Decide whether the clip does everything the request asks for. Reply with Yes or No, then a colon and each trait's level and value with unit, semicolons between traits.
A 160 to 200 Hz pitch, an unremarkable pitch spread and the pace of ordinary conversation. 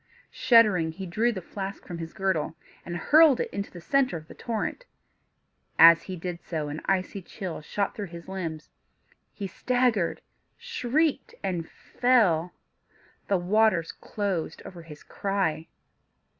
Yes: high, 190 Hz; average, 4.7 semitones; average, 145 wpm